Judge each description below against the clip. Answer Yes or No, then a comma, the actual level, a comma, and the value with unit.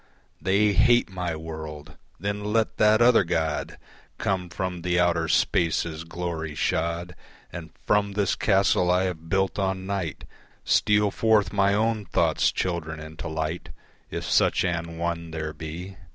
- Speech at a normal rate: Yes, average, 145 wpm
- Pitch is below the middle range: Yes, very low, 90 Hz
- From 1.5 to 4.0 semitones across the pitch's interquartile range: Yes, average, 3.5 semitones